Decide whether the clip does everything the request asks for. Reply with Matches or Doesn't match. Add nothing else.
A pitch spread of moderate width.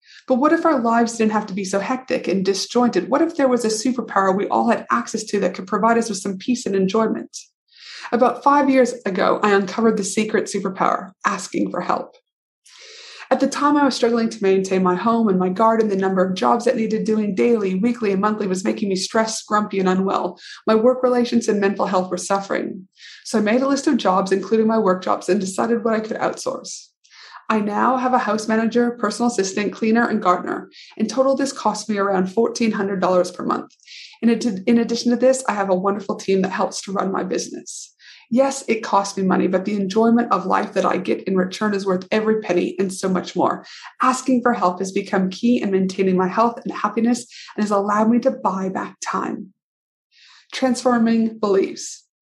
Matches